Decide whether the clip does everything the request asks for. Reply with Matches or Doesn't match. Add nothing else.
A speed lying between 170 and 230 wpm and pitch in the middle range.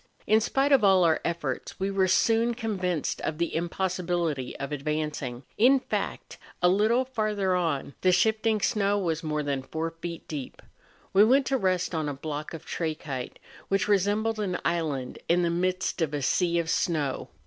Matches